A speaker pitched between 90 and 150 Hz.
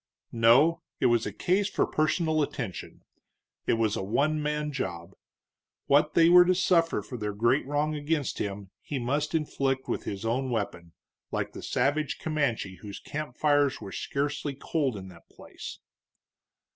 Yes: medium, 140 Hz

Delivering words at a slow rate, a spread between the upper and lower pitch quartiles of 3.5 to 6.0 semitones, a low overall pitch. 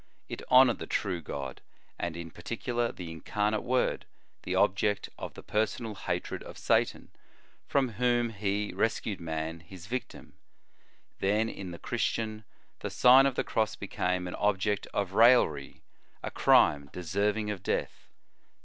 No: average, 145 wpm; average, 4.0 semitones; low, 105 Hz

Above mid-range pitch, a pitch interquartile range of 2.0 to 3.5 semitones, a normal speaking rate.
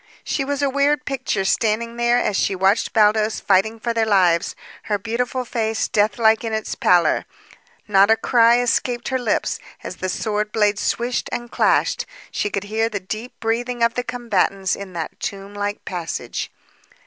Yes: high, 220 Hz; average, 2.8 semitones; average, 170 wpm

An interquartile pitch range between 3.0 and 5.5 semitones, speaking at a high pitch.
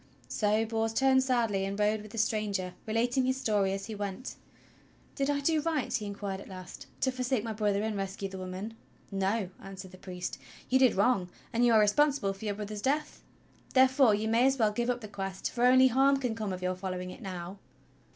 Yes: average, 4.4 semitones; high, 215 Hz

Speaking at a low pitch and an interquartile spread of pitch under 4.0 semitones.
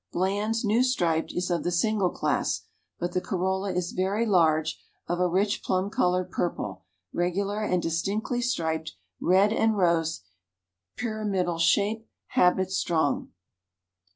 No: medium, 185 Hz; average, 3.1 semitones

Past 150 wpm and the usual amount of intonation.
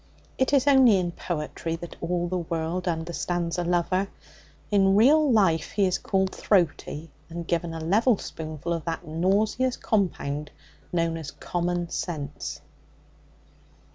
No: average, 140 wpm; average, 3.0 semitones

